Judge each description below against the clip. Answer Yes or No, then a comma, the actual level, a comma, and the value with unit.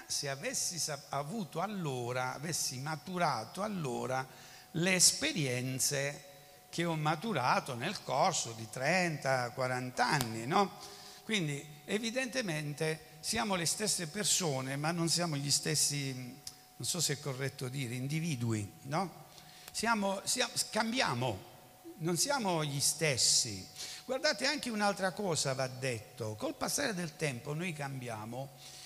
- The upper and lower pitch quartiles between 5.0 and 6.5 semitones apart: Yes, wide, 5.4 semitones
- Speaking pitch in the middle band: Yes, medium, 150 Hz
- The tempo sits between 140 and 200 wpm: No, slow, 115 wpm